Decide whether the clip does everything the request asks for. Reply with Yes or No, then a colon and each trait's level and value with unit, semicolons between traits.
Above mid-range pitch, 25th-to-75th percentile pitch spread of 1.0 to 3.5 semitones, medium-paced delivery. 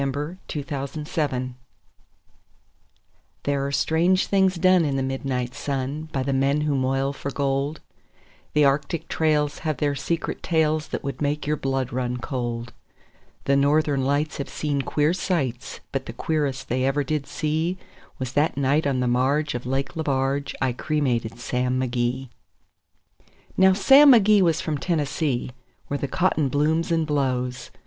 No: medium, 140 Hz; average, 2.7 semitones; average, 160 wpm